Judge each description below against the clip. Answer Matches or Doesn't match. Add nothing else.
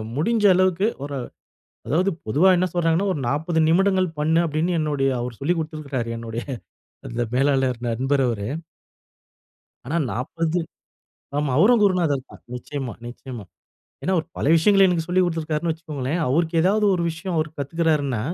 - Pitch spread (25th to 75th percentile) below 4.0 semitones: Doesn't match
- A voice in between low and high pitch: Matches